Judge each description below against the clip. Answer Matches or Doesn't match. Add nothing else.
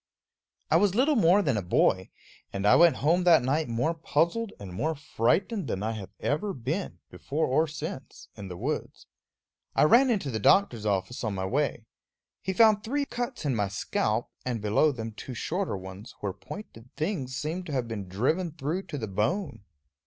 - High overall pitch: Doesn't match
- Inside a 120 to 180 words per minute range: Doesn't match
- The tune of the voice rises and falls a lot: Matches